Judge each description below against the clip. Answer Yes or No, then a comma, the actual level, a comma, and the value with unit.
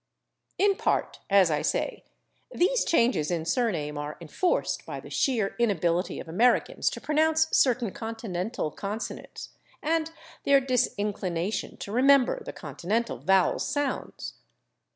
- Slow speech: Yes, slow, 125 wpm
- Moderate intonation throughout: No, wide, 7.5 semitones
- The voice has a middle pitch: No, high, 225 Hz